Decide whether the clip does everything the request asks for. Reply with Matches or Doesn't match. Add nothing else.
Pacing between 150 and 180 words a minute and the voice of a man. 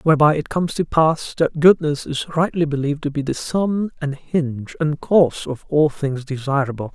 Doesn't match